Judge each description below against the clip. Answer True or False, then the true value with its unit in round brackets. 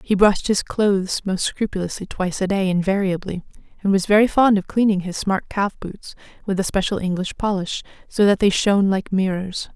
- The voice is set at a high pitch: True (195 Hz)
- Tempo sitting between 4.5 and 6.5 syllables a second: True (5.5 syllables/s)